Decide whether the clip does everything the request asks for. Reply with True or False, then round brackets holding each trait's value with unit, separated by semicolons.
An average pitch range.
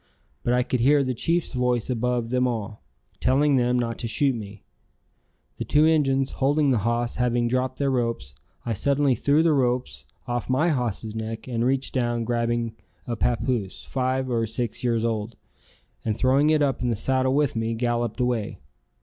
False (2.3 semitones)